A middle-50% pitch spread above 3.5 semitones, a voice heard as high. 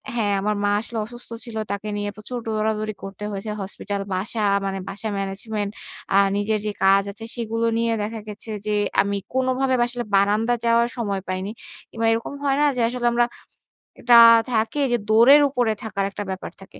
No: average, 2.7 semitones; high, 220 Hz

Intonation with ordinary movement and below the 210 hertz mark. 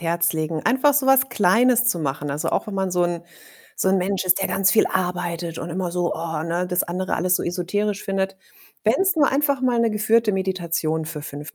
Yes: average, 4.0 semitones; medium, 185 Hz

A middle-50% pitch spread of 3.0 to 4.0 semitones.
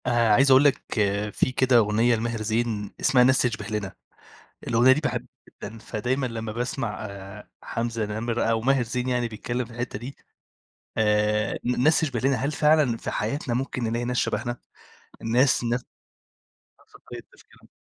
No: narrow, 2.5 semitones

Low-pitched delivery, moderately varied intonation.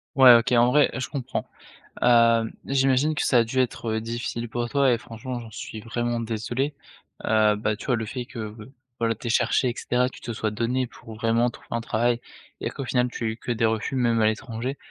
No: low, 120 Hz; narrow, 2.0 semitones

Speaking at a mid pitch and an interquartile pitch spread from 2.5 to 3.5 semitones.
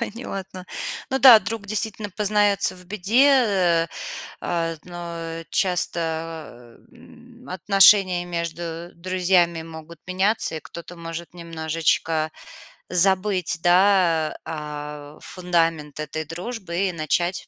Yes: medium, 175 Hz; average, 3.1 semitones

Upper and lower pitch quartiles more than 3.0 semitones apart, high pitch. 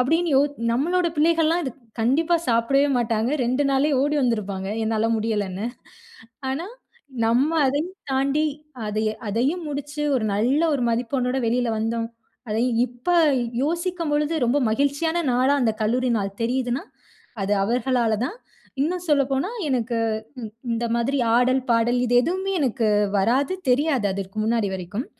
Yes: average, 4.2 semitones; very high, 250 Hz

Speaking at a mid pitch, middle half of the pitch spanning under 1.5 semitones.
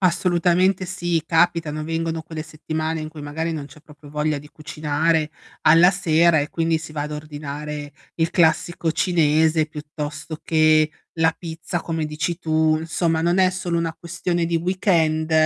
No: medium, 160 Hz; narrow, 1.8 semitones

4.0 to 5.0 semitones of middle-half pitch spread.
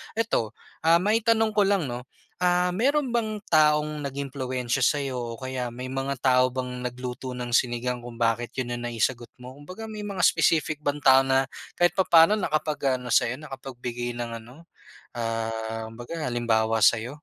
Yes: average, 4.7 semitones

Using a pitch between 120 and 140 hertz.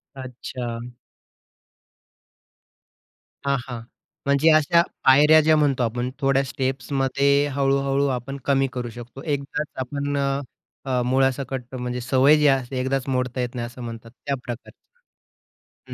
Yes: low, 135 Hz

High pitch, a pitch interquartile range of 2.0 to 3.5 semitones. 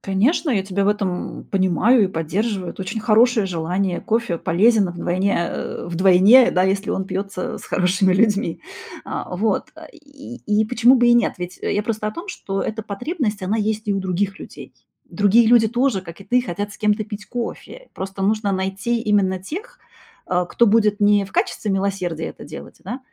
Yes: high, 205 Hz; average, 3.2 semitones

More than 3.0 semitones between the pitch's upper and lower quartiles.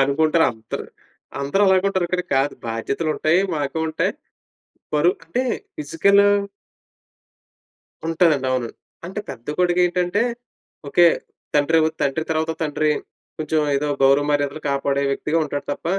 Yes: average, 3.8 semitones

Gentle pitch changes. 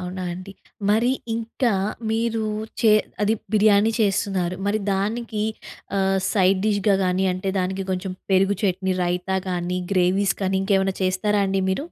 Yes: narrow, 2.2 semitones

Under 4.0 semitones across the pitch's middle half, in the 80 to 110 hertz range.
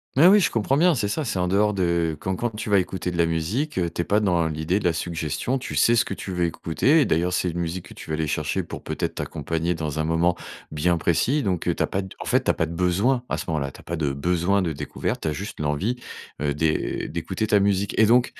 No: average, 4.3 semitones; very low, 90 Hz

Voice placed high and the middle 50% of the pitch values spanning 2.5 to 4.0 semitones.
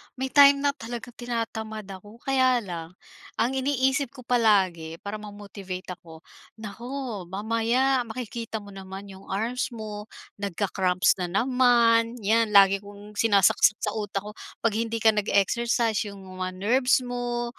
Yes: high, 220 Hz; average, 3.5 semitones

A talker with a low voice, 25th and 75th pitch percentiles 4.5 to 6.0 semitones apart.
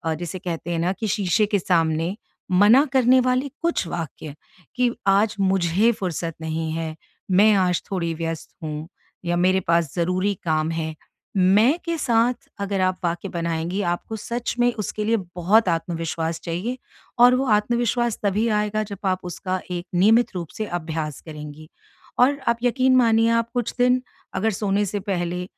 No: high, 190 Hz; average, 5.2 semitones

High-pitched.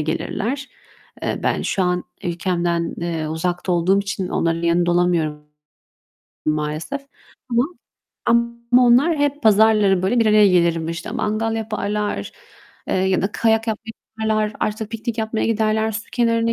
Yes: high, 210 Hz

